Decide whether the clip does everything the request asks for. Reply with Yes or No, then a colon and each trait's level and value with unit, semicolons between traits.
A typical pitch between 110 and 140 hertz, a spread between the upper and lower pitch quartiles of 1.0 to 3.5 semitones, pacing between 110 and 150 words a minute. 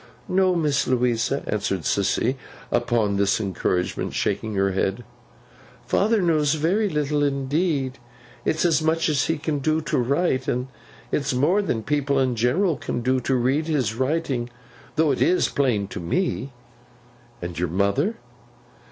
No: low, 135 Hz; average, 5.0 semitones; average, 145 wpm